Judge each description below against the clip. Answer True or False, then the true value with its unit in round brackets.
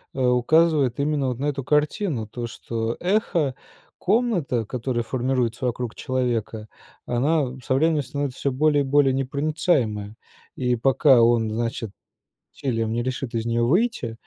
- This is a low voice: True (130 Hz)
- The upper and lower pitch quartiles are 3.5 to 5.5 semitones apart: True (3.9 semitones)